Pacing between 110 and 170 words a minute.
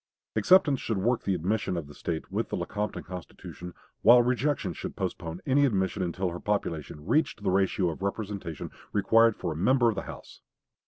No: average, 180 wpm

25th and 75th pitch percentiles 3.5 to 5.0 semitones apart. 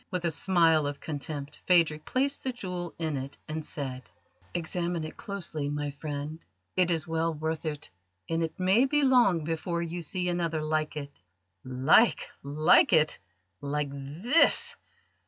No: average, 3.1 semitones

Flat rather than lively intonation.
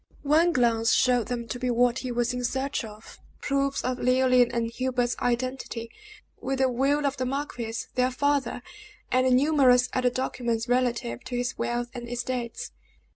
Yes: narrow, 1.5 semitones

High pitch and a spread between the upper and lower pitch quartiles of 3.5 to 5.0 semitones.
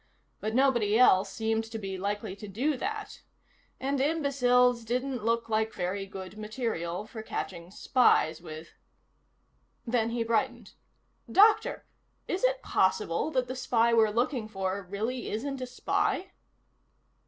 Yes: high, 225 Hz; average, 4.3 semitones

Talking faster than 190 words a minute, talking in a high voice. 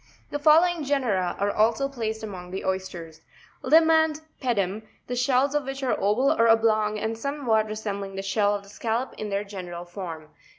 Yes: average, 200 wpm; high, 220 Hz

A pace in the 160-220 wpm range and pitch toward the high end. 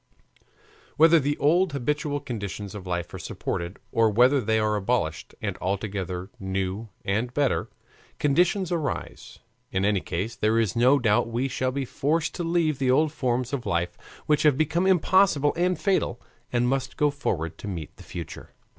No: average, 170 wpm; low, 125 Hz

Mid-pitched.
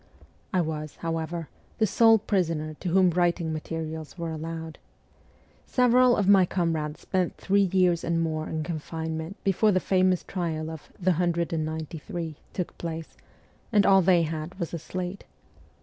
Yes: medium, 170 Hz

